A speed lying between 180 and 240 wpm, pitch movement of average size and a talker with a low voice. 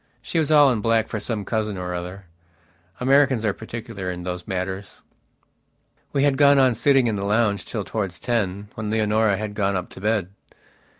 Yes: average, 185 wpm; average, 3.5 semitones; low, 110 Hz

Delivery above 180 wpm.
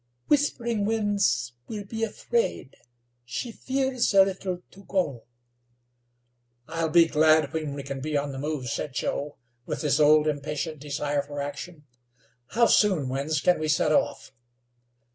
No: average, 145 wpm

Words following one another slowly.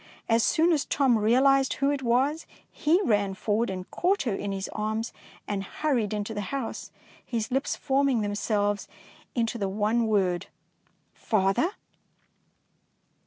No: average, 145 wpm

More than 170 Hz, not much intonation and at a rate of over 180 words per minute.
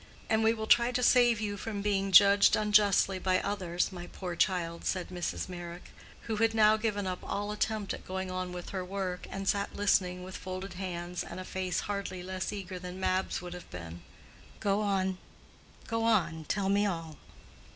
Yes: high, 190 Hz; narrow, 2.2 semitones; average, 190 wpm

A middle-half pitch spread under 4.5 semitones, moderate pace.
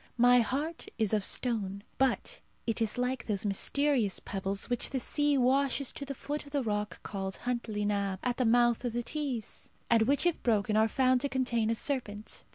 Yes: average, 4.0 semitones; average, 195 wpm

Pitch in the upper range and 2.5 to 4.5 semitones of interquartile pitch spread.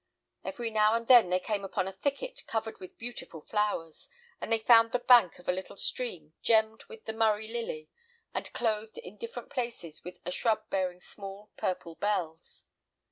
Yes: high, 215 Hz; average, 4.0 semitones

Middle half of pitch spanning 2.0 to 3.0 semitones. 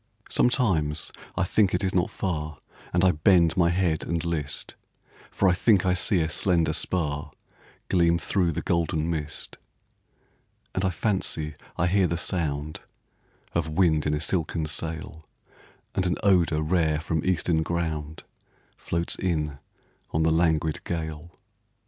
Yes: narrow, 2.6 semitones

